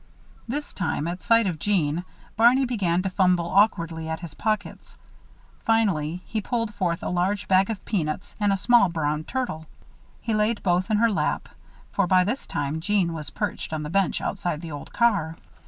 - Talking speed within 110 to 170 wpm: No, average, 185 wpm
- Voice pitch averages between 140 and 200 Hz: Yes, medium, 185 Hz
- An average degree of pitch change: Yes, average, 4.4 semitones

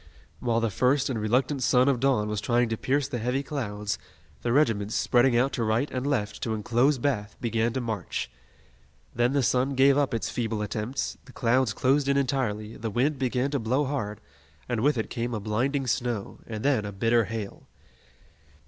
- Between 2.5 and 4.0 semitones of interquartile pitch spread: Yes, average, 3.4 semitones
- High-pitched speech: No, low, 120 Hz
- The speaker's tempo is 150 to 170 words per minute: No, average, 195 wpm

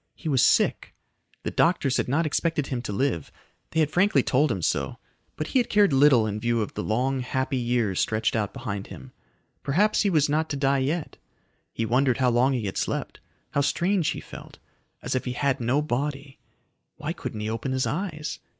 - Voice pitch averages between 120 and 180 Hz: Yes, low, 135 Hz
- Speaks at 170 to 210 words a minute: Yes, fast, 205 wpm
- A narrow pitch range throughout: No, average, 4.2 semitones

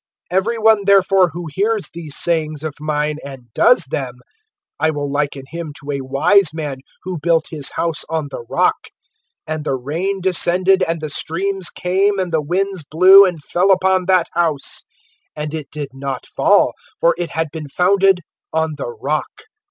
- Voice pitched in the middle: Yes, medium, 165 Hz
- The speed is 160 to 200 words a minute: Yes, average, 175 wpm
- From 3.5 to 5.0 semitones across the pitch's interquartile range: Yes, average, 4.1 semitones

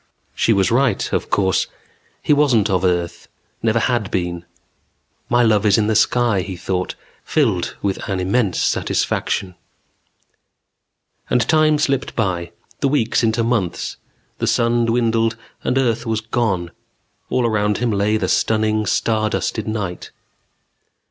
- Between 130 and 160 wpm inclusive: Yes, average, 140 wpm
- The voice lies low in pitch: Yes, low, 110 Hz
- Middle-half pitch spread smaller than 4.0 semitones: Yes, average, 3.6 semitones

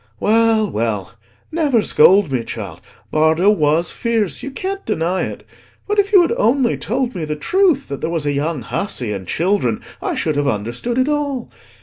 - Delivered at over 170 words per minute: Yes, average, 185 wpm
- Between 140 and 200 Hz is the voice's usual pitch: Yes, high, 190 Hz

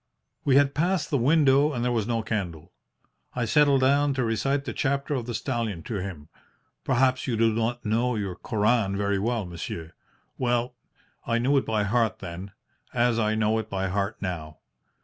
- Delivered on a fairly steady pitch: No, average, 4.4 semitones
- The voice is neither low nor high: No, low, 115 Hz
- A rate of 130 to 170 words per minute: No, average, 185 wpm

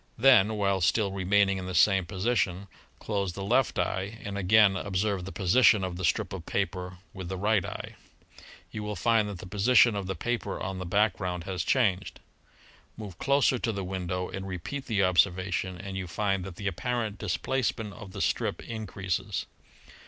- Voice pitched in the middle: No, low, 100 Hz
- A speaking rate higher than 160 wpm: Yes, average, 180 wpm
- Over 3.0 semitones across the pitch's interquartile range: No, narrow, 2.6 semitones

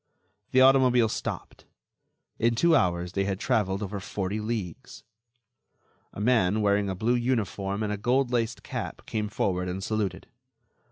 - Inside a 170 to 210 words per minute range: No, average, 145 wpm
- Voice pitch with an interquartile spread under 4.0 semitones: Yes, average, 3.6 semitones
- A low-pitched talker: Yes, low, 105 Hz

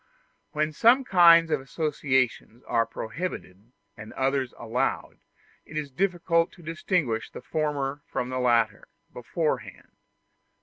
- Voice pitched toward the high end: No, medium, 140 Hz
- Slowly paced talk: Yes, slow, 120 wpm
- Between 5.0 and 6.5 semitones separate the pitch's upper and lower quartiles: Yes, average, 5.3 semitones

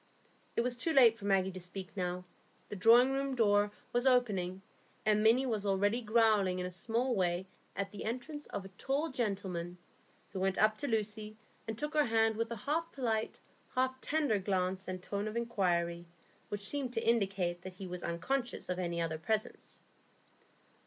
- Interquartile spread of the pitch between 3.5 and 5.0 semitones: Yes, average, 4.4 semitones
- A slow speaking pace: No, average, 180 wpm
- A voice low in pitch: No, high, 210 Hz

